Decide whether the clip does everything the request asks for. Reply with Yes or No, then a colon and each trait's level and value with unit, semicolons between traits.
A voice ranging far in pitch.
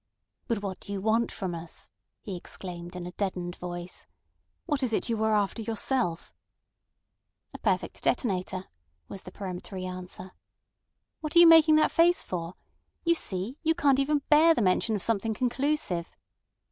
Yes: wide, 7.1 semitones